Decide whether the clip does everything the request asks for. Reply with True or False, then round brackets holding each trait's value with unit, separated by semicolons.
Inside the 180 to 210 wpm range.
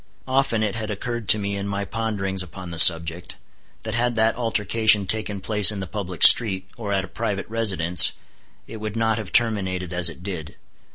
True (190 wpm)